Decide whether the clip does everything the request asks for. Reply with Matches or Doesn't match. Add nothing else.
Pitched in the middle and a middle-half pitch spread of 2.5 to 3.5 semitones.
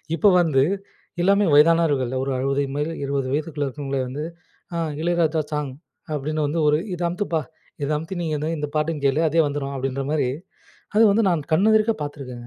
Matches